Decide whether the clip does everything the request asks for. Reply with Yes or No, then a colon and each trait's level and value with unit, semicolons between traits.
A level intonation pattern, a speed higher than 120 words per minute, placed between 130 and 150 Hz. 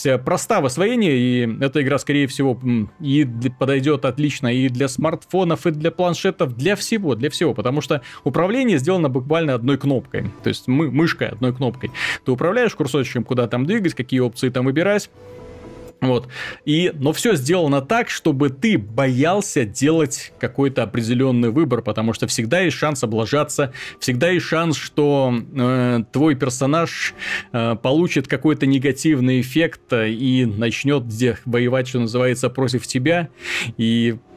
No: average, 4.2 semitones; average, 145 wpm; medium, 140 Hz